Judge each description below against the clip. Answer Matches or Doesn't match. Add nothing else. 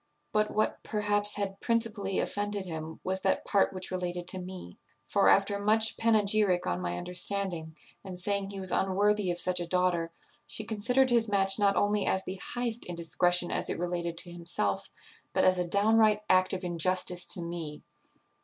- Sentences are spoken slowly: Doesn't match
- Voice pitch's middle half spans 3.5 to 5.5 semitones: Doesn't match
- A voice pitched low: Doesn't match